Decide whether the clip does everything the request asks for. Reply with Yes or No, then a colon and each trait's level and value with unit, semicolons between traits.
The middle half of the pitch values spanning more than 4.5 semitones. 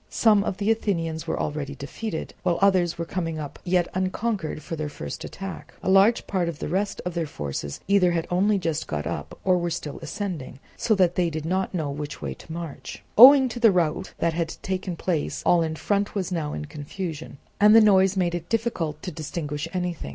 No: average, 3.5 semitones